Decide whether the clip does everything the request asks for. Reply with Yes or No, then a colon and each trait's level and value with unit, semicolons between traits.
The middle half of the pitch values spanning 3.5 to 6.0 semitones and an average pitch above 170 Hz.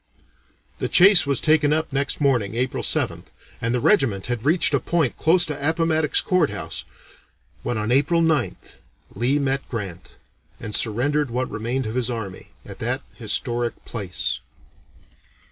No: average, 4.9 semitones; low, 130 Hz